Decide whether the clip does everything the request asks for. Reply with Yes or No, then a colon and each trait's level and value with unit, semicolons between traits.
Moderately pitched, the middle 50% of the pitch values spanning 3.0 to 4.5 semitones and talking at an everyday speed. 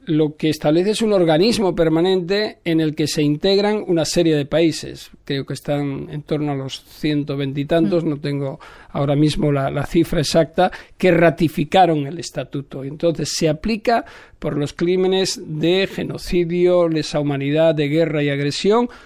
Yes: medium, 160 Hz; average, 3.3 semitones; average, 160 wpm